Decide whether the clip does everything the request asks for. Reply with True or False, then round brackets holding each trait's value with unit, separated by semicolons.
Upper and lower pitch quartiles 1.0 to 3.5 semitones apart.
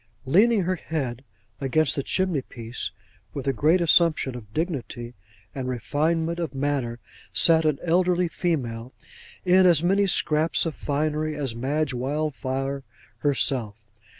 False (4.2 semitones)